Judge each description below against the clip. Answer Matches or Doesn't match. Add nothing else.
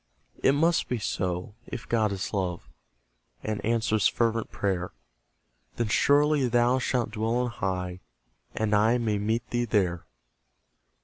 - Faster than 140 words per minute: Doesn't match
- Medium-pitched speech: Doesn't match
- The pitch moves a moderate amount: Matches